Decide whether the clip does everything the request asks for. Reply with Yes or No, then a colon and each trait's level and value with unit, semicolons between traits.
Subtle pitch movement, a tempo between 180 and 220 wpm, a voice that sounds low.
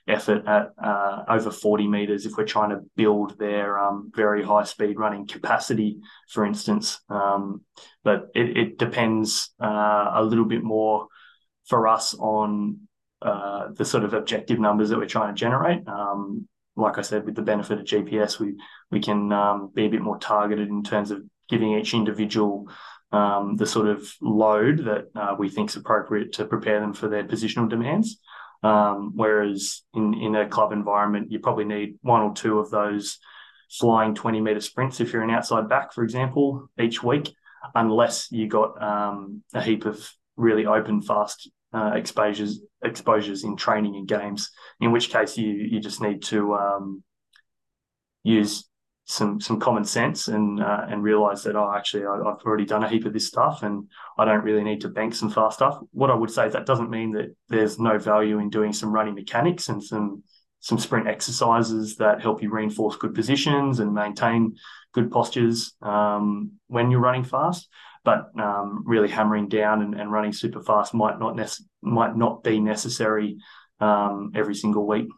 Yes: narrow, 1.2 semitones; average, 185 wpm; low, 105 Hz